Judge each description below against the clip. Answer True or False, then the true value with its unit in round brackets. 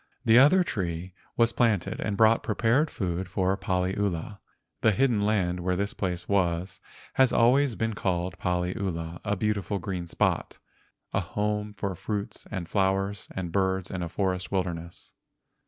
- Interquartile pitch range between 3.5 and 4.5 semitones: False (2.9 semitones)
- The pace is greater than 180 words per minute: False (150 wpm)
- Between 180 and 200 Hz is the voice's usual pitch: False (95 Hz)